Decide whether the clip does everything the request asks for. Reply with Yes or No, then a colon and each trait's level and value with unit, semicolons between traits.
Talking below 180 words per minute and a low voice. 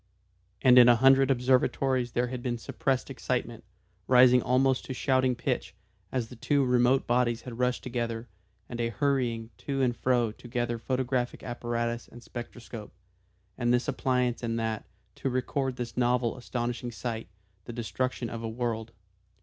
Yes: average, 160 wpm; low, 125 Hz